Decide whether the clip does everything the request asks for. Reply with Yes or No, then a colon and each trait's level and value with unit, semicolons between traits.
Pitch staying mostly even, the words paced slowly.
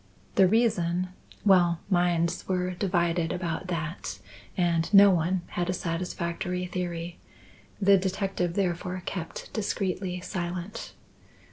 Yes: narrow, 1.7 semitones; slow, 110 wpm